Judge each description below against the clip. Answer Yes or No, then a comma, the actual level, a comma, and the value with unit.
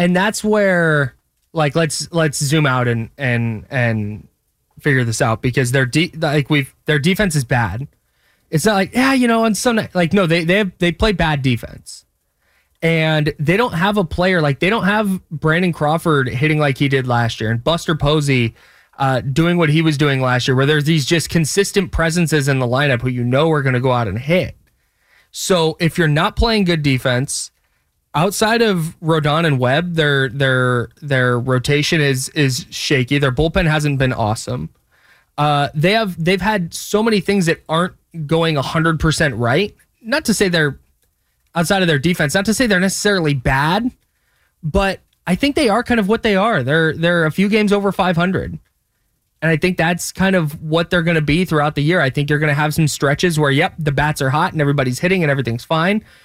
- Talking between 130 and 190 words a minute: No, fast, 205 wpm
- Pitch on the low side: No, medium, 160 Hz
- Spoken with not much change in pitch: No, average, 4.7 semitones